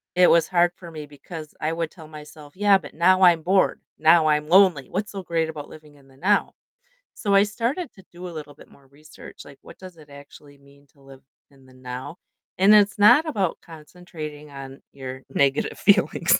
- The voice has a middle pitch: Yes, medium, 155 Hz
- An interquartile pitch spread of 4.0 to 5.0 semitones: Yes, average, 4.4 semitones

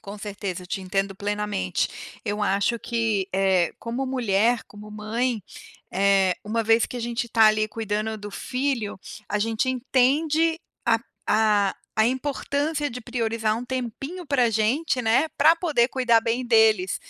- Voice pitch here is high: Yes, high, 225 Hz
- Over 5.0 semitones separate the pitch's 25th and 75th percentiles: No, average, 3.5 semitones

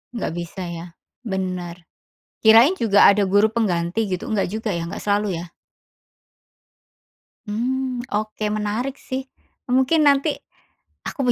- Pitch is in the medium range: No, high, 215 Hz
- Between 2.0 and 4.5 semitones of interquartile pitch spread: No, average, 5.0 semitones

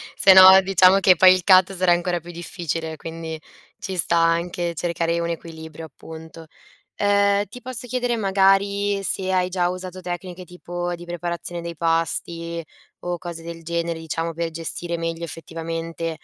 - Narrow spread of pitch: Yes, narrow, 2.0 semitones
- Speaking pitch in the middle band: Yes, medium, 175 Hz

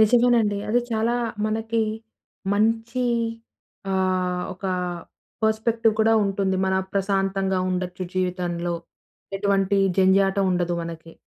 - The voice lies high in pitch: Yes, high, 195 Hz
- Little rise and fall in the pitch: No, average, 3.0 semitones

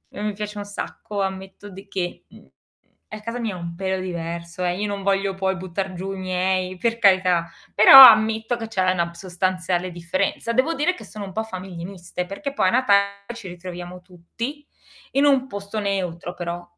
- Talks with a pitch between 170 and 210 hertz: Yes, high, 190 Hz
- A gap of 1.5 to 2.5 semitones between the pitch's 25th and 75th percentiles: No, average, 2.9 semitones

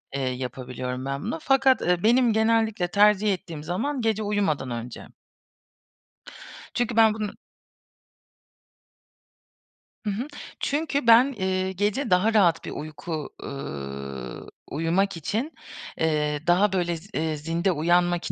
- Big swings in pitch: Yes, wide, 6.3 semitones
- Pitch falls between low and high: Yes, medium, 180 Hz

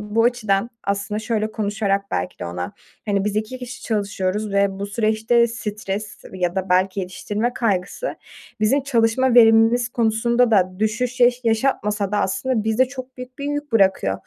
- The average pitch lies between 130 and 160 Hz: No, high, 215 Hz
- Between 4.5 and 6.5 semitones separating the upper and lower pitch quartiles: No, average, 3.3 semitones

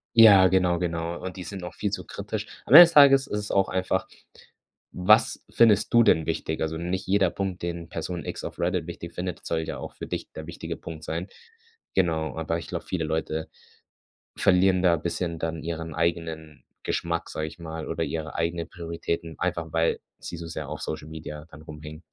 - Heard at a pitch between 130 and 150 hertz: No, very low, 85 Hz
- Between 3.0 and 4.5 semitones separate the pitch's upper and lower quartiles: No, narrow, 2.4 semitones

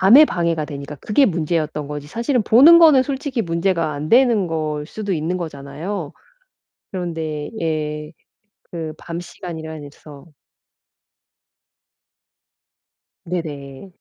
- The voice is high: No, medium, 165 Hz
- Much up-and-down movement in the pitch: No, average, 4.7 semitones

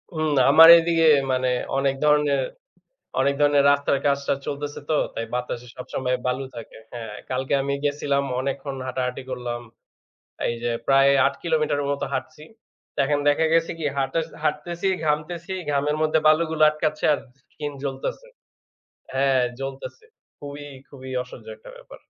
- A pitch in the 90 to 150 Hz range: Yes, medium, 140 Hz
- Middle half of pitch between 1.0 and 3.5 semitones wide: Yes, narrow, 2.4 semitones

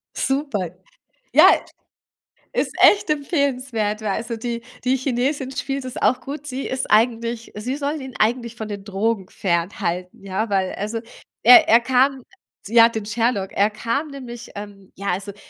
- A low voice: No, high, 230 Hz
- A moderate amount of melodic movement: Yes, average, 4.2 semitones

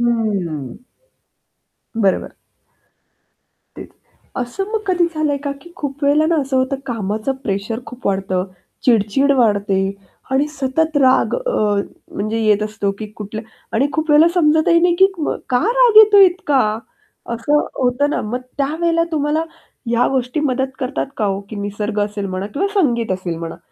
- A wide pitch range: Yes, wide, 6.6 semitones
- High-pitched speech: Yes, very high, 260 Hz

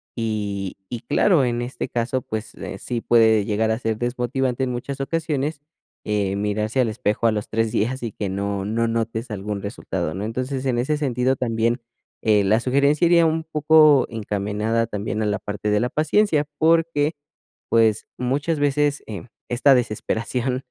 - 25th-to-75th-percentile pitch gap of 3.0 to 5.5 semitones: Yes, average, 4.2 semitones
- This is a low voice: Yes, low, 120 Hz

